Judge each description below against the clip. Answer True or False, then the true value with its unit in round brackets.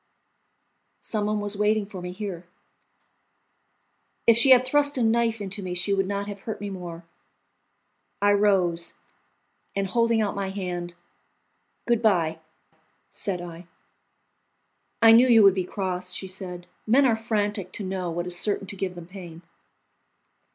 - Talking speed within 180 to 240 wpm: False (150 wpm)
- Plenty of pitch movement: False (3.2 semitones)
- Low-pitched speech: False (195 Hz)